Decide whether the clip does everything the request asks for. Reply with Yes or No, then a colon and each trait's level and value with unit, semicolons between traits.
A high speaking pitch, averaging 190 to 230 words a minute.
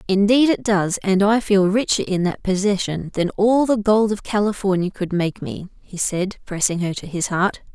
Yes: high, 195 Hz; average, 200 wpm